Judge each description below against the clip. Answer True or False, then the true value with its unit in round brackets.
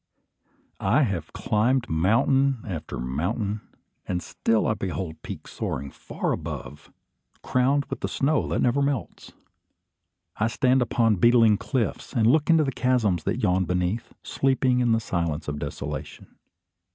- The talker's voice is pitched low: True (115 Hz)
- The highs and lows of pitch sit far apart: True (6.2 semitones)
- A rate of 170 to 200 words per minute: False (140 wpm)